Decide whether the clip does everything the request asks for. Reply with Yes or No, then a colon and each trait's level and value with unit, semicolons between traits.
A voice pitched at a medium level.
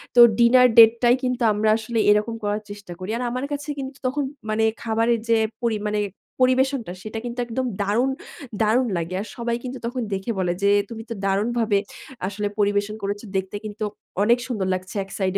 No: high, 225 Hz